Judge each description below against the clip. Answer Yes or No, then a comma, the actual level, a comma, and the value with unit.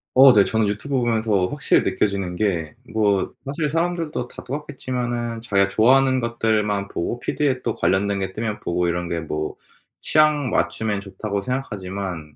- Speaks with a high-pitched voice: No, low, 110 Hz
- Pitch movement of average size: Yes, average, 4.6 semitones